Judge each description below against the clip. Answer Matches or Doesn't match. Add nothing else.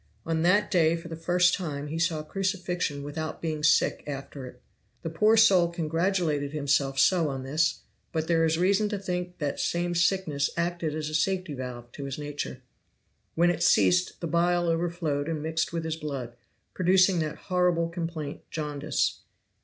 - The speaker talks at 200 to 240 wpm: Doesn't match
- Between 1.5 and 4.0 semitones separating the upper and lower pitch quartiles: Matches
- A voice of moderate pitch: Matches